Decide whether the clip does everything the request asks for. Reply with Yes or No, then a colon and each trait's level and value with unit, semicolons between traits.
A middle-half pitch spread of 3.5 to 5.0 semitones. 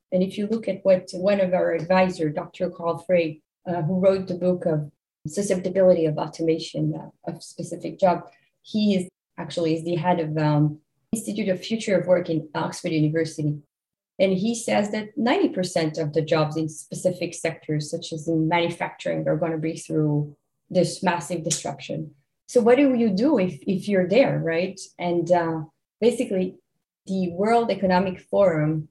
No: average, 2.8 semitones